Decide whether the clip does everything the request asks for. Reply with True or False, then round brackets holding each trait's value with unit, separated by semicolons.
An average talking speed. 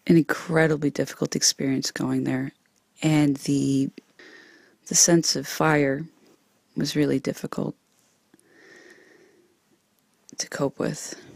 False (95 wpm)